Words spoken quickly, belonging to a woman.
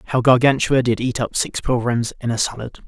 No: fast, 210 wpm; male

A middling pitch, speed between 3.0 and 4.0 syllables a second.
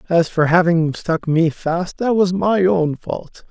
Yes: medium, 175 Hz; 3.7 syllables/s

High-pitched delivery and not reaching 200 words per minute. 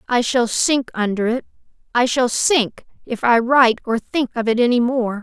Yes: high, 240 Hz; average, 185 wpm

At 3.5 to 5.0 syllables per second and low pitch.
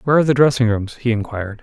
No: 7.8 syllables/s; low, 120 Hz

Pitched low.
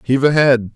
Yes: low, 130 Hz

